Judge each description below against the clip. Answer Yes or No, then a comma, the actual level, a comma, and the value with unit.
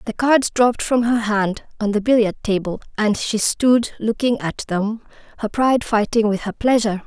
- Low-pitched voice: No, high, 220 Hz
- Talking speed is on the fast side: No, average, 185 wpm